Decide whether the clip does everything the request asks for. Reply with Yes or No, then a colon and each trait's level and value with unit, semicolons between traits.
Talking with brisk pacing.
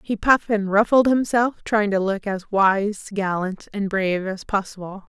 No: average, 175 wpm